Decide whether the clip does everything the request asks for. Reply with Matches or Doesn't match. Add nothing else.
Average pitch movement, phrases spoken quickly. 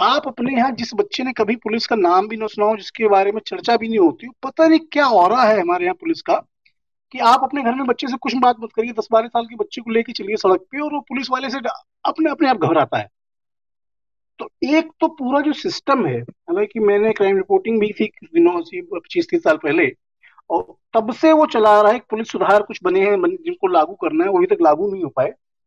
Doesn't match